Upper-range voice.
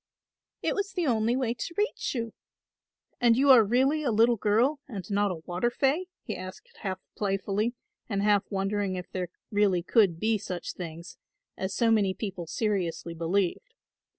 Yes: high, 205 Hz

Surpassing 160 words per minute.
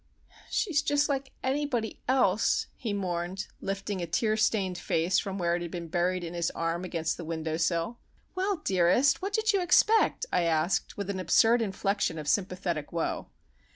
Yes: average, 175 wpm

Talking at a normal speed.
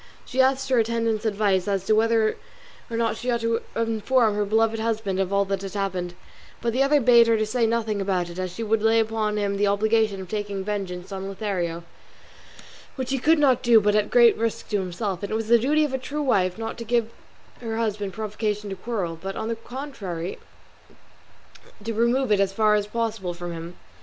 No: fast, 210 wpm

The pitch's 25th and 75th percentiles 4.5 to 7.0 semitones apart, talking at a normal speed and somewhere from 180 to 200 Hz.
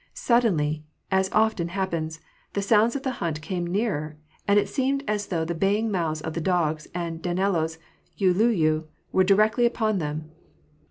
Yes: average, 4.9 semitones; average, 160 wpm; medium, 185 Hz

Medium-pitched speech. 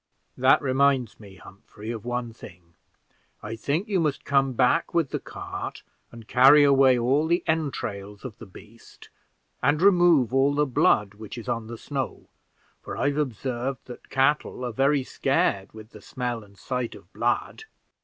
No: low, 125 Hz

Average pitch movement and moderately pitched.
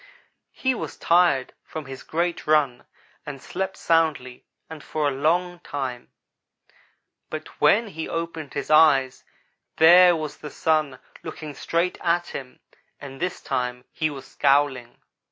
Yes: average, 3.9 semitones; medium, 155 Hz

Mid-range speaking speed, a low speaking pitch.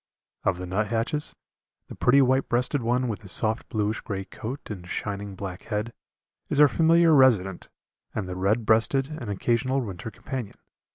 Yes: average, 165 wpm; low, 115 Hz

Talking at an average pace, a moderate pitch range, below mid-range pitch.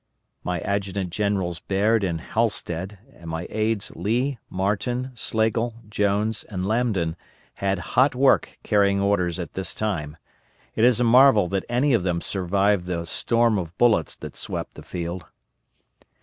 Yes: average, 150 wpm; average, 4.0 semitones; low, 100 Hz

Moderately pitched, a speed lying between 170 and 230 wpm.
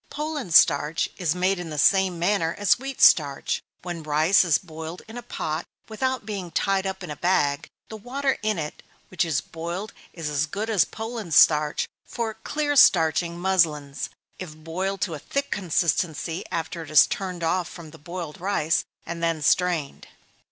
Yes: medium, 175 Hz; average, 175 wpm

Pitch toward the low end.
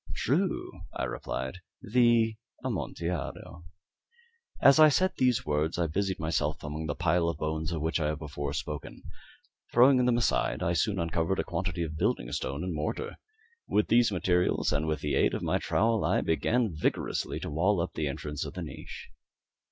Yes: very low, 85 Hz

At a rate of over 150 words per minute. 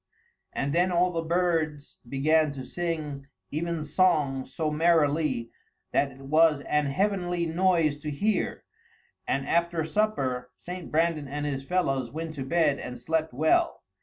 No: average, 140 wpm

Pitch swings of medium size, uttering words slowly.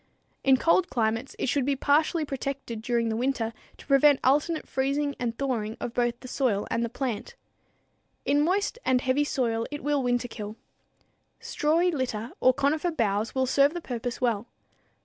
No: average, 3.6 semitones; average, 170 wpm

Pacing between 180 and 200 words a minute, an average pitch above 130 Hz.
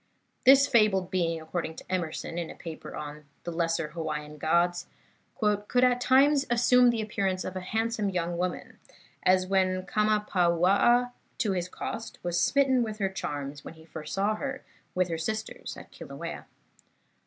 No: average, 160 wpm; medium, 185 Hz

